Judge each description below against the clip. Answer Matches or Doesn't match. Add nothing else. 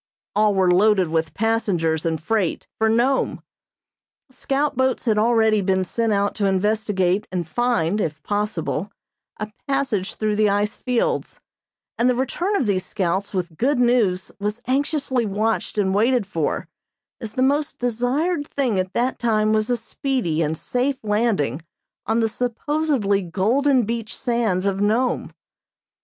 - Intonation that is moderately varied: Matches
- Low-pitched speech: Doesn't match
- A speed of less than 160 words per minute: Matches